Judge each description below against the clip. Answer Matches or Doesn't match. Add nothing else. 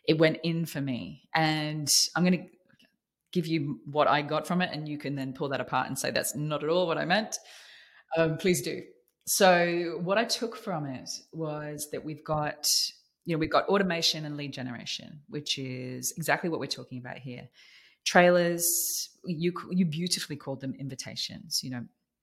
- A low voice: Doesn't match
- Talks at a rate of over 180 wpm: Matches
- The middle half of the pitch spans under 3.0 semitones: Doesn't match